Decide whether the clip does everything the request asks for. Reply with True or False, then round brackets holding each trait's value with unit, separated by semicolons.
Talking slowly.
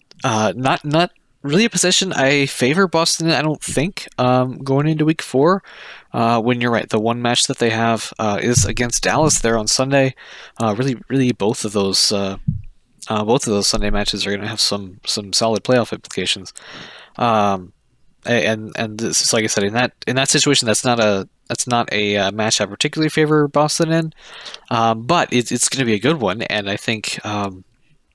False (205 wpm)